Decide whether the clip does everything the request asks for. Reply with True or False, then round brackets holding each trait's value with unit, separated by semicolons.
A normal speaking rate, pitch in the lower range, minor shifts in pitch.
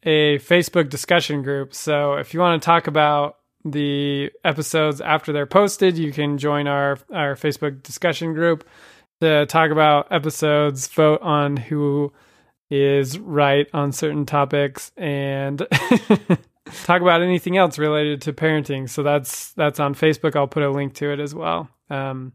False (155 wpm; 150 Hz; 2.1 semitones)